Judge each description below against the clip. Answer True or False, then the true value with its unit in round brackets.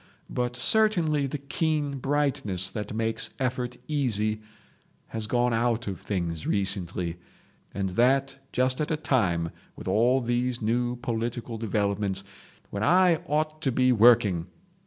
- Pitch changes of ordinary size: True (4.7 semitones)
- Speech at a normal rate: False (130 wpm)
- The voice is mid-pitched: False (120 Hz)